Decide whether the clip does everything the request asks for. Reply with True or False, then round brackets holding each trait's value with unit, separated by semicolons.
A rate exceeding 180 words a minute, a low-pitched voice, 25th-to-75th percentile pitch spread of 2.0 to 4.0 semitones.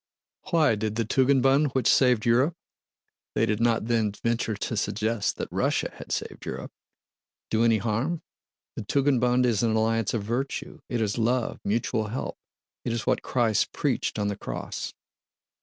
False (160 wpm; 115 Hz; 2.5 semitones)